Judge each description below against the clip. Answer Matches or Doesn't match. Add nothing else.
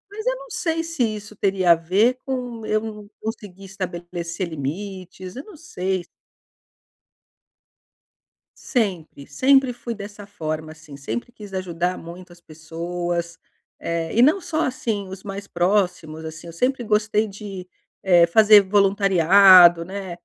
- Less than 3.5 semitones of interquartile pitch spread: Doesn't match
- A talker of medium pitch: Doesn't match